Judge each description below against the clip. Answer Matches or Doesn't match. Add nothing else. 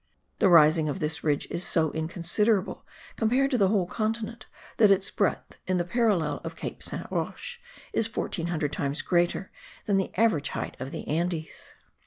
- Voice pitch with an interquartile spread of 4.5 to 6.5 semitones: Matches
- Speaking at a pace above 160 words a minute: Matches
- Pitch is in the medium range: Matches